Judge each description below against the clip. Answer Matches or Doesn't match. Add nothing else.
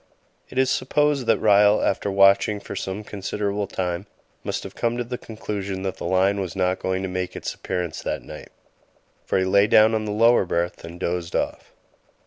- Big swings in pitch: Doesn't match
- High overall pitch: Doesn't match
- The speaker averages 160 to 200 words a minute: Matches